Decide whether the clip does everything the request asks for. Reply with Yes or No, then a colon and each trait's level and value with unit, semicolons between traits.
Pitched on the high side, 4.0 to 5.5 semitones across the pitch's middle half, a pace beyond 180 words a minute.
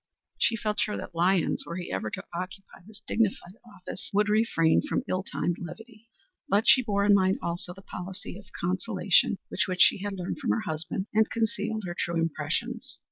No: high, 195 Hz; average, 3.4 semitones; average, 190 wpm